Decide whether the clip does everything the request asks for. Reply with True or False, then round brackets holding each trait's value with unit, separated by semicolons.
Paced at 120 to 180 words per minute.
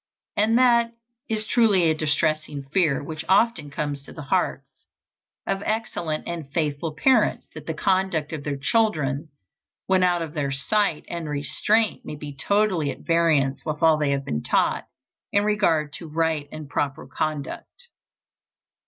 True (155 wpm)